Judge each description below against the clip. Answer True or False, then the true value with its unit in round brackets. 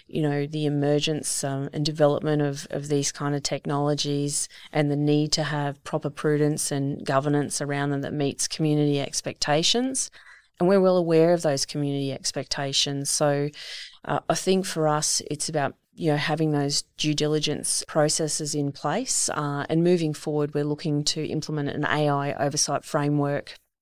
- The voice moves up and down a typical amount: False (1.3 semitones)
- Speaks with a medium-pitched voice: True (150 Hz)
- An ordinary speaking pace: True (165 wpm)